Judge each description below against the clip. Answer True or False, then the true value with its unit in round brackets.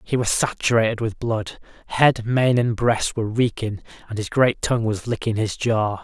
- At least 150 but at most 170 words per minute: False (190 wpm)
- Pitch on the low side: True (115 Hz)